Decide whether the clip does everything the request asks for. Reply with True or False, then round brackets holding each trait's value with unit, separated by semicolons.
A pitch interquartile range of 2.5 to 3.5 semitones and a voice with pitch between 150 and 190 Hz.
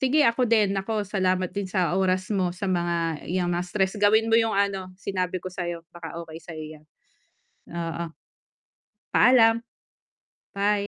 True (3.0 semitones; 185 Hz)